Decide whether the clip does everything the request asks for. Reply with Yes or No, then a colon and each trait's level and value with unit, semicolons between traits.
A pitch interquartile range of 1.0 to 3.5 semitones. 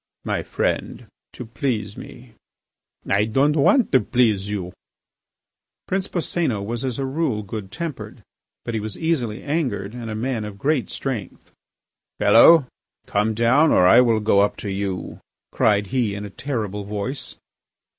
No: average, 4.6 semitones